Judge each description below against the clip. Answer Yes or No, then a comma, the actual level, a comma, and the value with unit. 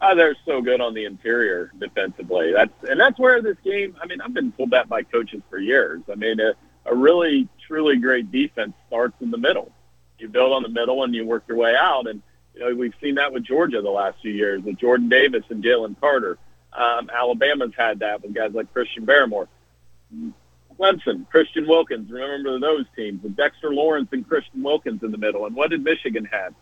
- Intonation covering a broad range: Yes, wide, 7.5 semitones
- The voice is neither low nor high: No, low, 130 Hz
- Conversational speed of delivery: No, fast, 210 wpm